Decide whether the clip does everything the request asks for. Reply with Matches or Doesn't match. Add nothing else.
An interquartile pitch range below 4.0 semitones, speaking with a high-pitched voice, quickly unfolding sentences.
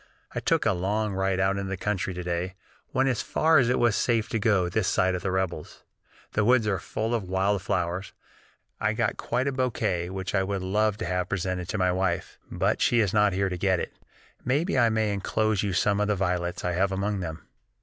Doesn't match